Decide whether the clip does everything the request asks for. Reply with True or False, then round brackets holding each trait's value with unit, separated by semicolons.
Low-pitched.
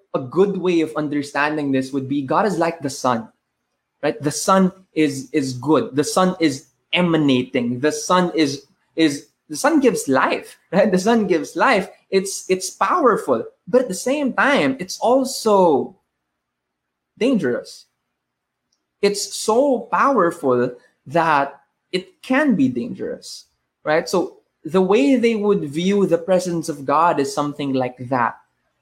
False (170 Hz)